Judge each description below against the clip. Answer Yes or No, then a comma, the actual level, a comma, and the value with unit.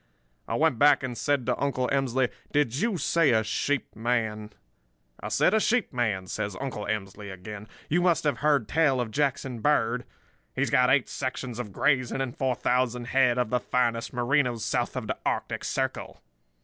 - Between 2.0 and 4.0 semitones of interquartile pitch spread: Yes, average, 3.7 semitones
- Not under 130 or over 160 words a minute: No, average, 180 wpm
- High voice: No, low, 125 Hz